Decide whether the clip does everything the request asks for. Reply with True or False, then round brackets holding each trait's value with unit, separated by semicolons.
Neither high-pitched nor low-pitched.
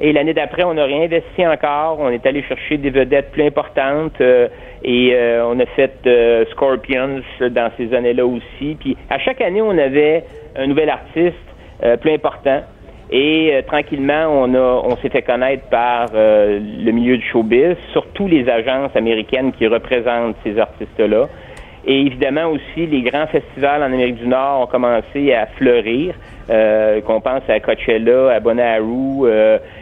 False (130 Hz)